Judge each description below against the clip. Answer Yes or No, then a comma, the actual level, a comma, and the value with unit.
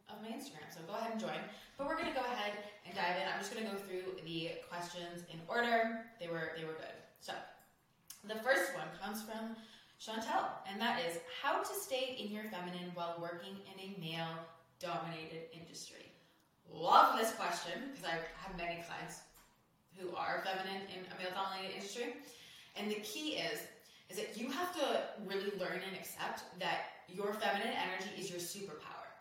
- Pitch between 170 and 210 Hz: Yes, high, 190 Hz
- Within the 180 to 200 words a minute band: Yes, average, 185 wpm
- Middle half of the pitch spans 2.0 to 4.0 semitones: No, average, 4.6 semitones